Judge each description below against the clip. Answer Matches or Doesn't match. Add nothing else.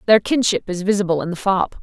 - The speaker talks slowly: Doesn't match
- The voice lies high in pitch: Matches